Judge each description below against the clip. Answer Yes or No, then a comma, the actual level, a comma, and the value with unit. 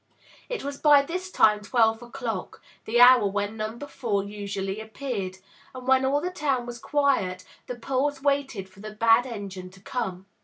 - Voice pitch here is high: Yes, high, 235 Hz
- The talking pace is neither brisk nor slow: Yes, average, 175 wpm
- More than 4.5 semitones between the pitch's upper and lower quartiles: Yes, average, 5.1 semitones